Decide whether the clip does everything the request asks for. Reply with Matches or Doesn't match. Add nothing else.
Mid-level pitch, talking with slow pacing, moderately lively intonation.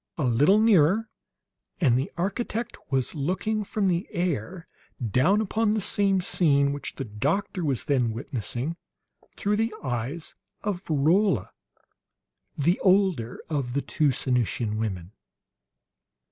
Doesn't match